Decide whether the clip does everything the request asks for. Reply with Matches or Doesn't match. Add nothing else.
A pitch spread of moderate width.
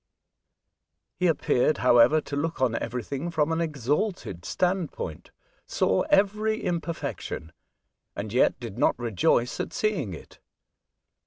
Doesn't match